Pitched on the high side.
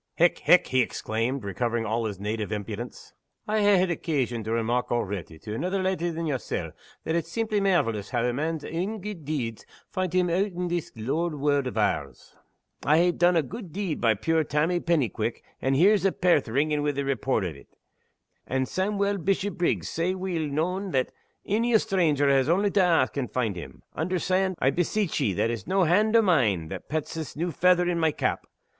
No: medium, 160 Hz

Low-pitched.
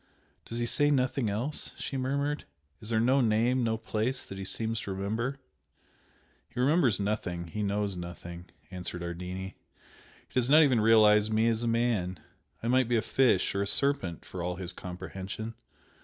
Yes: low, 110 Hz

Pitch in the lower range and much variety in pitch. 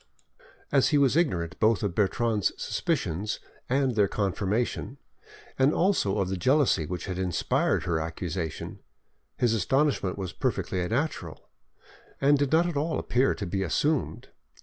Yes: low, 110 Hz; wide, 7.1 semitones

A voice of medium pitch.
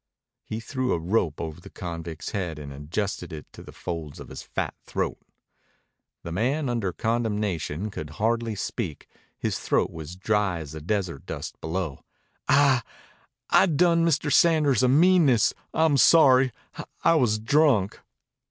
No: low, 105 Hz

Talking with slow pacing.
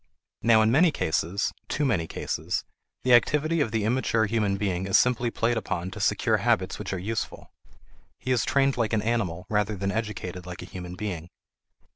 No: average, 185 wpm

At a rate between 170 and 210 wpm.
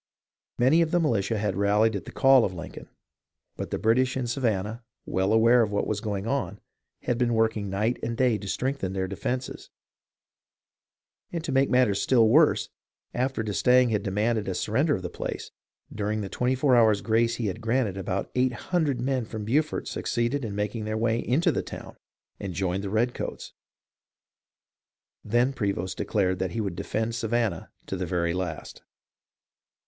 Yes: average, 180 wpm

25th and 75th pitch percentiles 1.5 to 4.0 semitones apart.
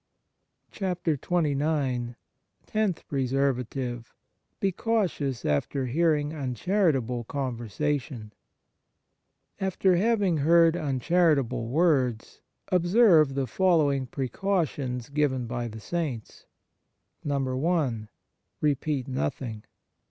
No: average, 5.2 semitones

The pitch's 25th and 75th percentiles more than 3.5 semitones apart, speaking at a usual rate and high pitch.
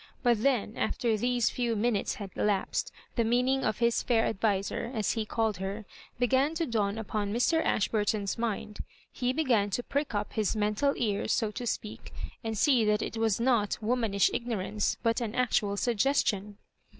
No: average, 2.8 semitones; average, 170 wpm; high, 225 Hz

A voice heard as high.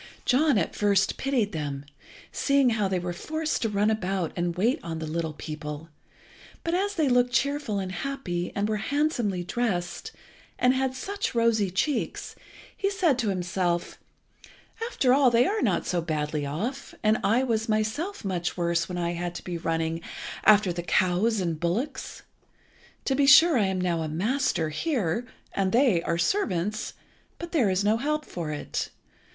Yes: high, 205 Hz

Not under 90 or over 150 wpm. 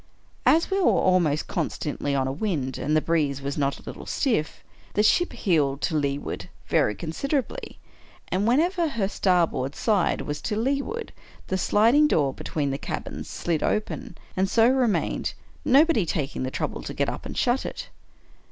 No: average, 170 wpm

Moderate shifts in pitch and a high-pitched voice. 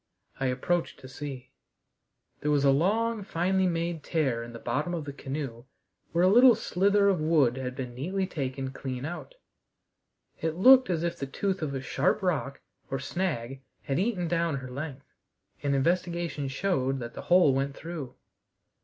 No: average, 5.0 semitones; medium, 155 Hz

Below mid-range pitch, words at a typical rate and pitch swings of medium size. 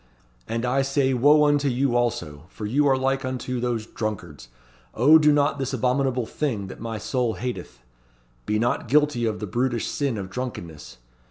Yes: low, 125 Hz; average, 175 wpm; average, 3.8 semitones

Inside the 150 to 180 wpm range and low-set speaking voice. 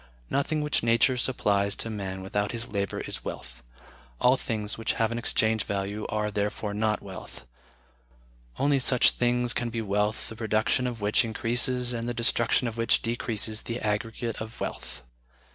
Yes: average, 165 wpm; low, 110 Hz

